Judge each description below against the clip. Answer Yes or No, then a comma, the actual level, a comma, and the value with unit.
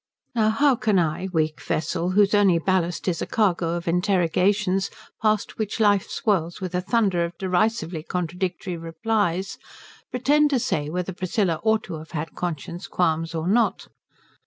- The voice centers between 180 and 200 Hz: Yes, medium, 185 Hz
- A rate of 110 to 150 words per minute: No, average, 160 wpm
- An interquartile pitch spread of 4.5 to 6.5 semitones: No, average, 3.7 semitones